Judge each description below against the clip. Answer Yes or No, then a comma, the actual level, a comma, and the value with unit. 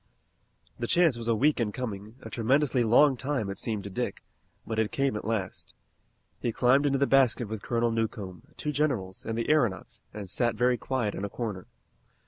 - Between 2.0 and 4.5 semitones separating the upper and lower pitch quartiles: Yes, average, 3.8 semitones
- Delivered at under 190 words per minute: No, average, 195 wpm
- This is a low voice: Yes, low, 115 Hz